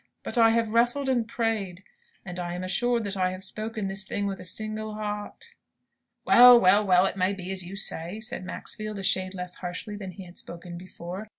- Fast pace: Yes, fast, 210 wpm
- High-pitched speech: Yes, high, 195 Hz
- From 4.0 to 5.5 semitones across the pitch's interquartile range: No, average, 3.0 semitones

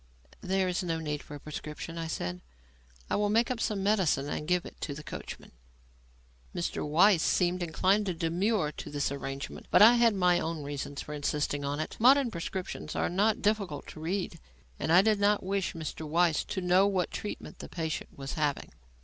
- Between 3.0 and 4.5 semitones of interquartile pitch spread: No, average, 4.9 semitones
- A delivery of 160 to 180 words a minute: No, average, 195 wpm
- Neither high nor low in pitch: Yes, medium, 175 Hz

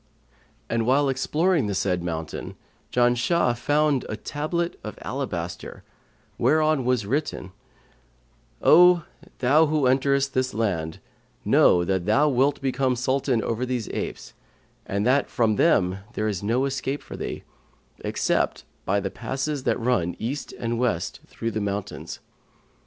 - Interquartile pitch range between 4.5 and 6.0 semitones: Yes, average, 5.0 semitones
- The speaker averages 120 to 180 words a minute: Yes, slow, 135 wpm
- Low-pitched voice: Yes, low, 125 Hz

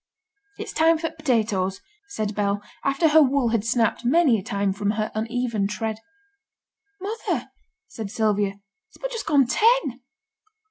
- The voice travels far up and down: Yes, wide, 6.7 semitones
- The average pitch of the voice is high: Yes, high, 230 Hz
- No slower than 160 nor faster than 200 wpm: No, average, 150 wpm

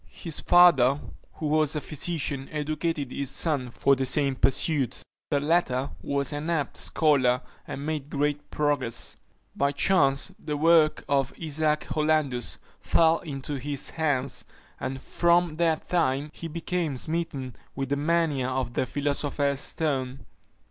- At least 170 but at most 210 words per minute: No, average, 140 wpm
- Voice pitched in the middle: Yes, medium, 145 Hz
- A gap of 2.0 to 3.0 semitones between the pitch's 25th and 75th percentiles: Yes, narrow, 2.6 semitones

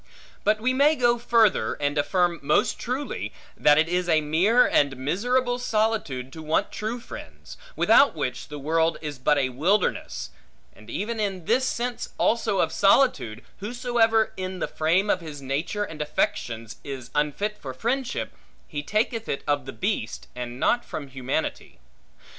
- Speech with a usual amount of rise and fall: No, wide, 7.8 semitones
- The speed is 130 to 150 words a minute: No, average, 160 wpm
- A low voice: No, medium, 175 Hz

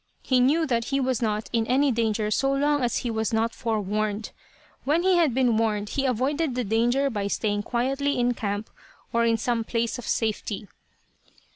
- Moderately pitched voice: No, high, 235 Hz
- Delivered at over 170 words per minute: Yes, average, 185 wpm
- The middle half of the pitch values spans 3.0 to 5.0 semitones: Yes, average, 3.3 semitones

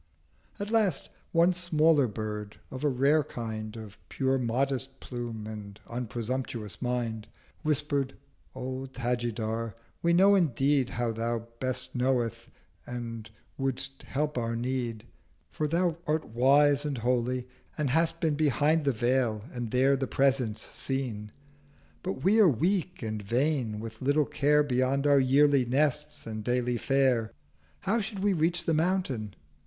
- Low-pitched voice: Yes, low, 130 Hz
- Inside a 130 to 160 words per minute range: Yes, average, 140 wpm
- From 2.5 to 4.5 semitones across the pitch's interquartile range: Yes, average, 4.2 semitones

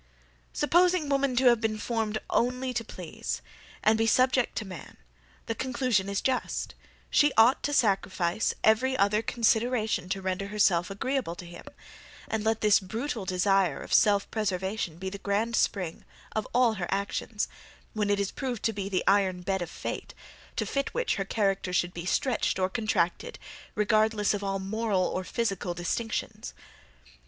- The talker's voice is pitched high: Yes, high, 210 Hz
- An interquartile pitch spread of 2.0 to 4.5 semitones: Yes, average, 3.5 semitones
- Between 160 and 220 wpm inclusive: Yes, average, 165 wpm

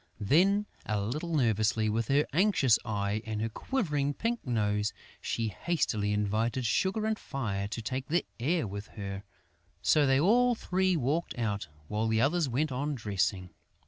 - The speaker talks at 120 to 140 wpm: No, average, 160 wpm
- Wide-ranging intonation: Yes, wide, 7.3 semitones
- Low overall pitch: Yes, low, 120 Hz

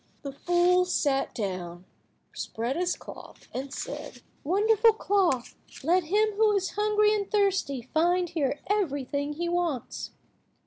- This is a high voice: Yes, very high, 350 Hz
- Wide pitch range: Yes, wide, 6.4 semitones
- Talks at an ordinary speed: No, slow, 130 wpm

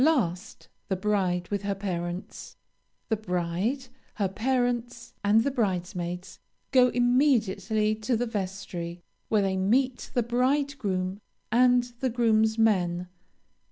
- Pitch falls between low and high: No, high, 215 Hz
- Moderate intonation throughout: Yes, average, 4.8 semitones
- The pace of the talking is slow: Yes, slow, 115 wpm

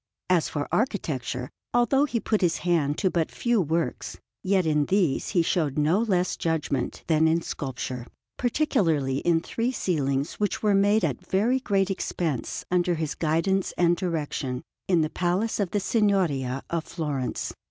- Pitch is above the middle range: No, medium, 170 Hz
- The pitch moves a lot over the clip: No, average, 4.8 semitones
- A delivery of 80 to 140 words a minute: No, average, 160 wpm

